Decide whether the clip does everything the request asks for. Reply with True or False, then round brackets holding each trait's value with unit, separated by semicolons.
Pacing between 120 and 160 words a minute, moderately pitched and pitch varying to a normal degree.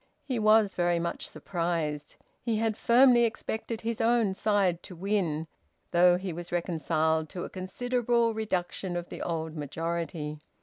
True (145 wpm; 180 Hz; 4.7 semitones)